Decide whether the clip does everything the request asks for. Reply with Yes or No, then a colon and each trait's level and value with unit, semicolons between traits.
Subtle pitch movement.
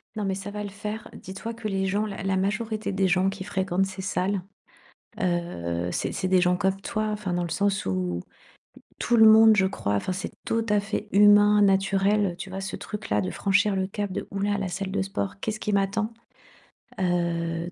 Yes: narrow, 2.1 semitones